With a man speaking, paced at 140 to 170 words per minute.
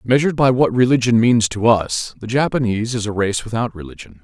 No: male; average, 200 wpm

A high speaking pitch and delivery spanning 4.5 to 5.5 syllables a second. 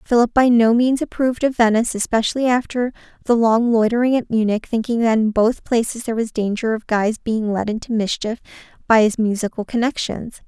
No: high, 230 Hz; 5.7 syllables/s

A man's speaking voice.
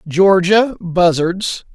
Yes: male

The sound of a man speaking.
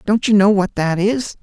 Yes: male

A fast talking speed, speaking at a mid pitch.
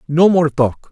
No: average, 195 wpm; medium, 155 Hz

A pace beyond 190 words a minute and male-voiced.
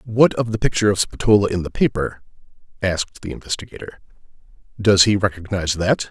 No: average, 155 wpm; male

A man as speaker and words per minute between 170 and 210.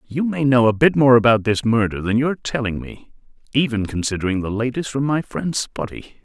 Yes: male; average, 200 wpm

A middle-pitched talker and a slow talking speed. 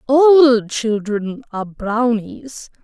No: high, 235 Hz; slow, 85 wpm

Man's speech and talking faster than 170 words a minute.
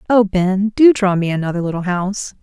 No: female; average, 200 wpm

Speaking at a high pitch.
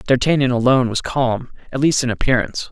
No: low, 130 Hz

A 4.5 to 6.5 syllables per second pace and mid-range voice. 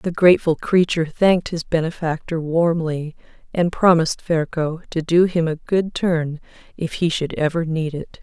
Yes: 4.7 syllables/s; medium, 165 Hz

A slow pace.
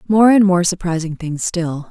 No: average, 190 wpm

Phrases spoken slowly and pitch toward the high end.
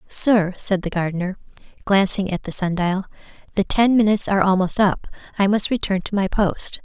No: average, 185 wpm; high, 195 Hz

